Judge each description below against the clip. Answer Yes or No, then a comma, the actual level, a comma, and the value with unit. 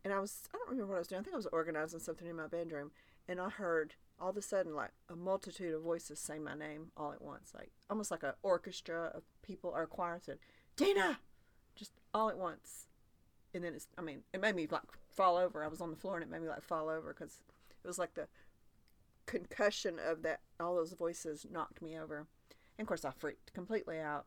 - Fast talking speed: Yes, fast, 240 wpm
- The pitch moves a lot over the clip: No, average, 3.2 semitones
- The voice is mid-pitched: Yes, medium, 170 Hz